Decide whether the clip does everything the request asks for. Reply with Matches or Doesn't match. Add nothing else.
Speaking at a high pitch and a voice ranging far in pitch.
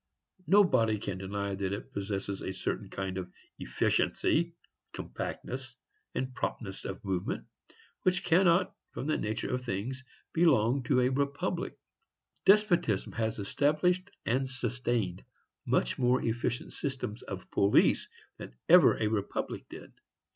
Doesn't match